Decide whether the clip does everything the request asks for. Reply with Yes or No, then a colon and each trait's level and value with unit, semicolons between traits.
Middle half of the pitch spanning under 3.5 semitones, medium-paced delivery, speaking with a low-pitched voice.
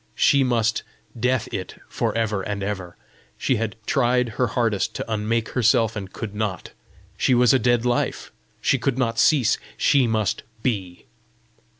Yes: average, 2.9 semitones; average, 160 wpm; low, 115 Hz